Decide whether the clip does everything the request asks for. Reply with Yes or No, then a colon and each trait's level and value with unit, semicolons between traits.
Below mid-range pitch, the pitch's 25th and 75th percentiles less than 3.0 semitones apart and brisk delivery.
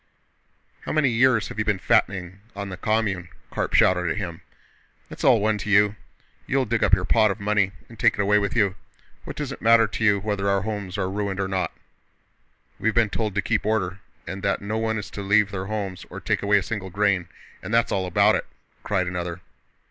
Yes: low, 100 Hz; narrow, 2.4 semitones; fast, 220 wpm